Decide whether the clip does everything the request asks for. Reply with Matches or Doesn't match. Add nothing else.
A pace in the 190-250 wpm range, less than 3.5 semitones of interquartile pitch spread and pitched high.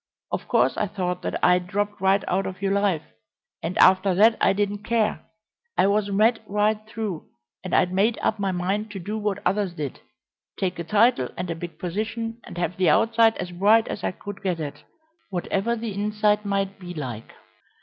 Matches